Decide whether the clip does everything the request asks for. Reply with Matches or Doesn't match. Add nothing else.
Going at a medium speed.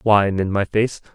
Doesn't match